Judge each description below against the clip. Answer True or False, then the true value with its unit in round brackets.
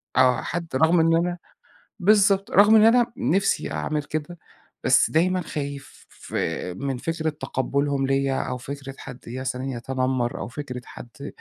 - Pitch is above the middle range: False (145 Hz)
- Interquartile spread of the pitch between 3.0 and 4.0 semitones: False (4.9 semitones)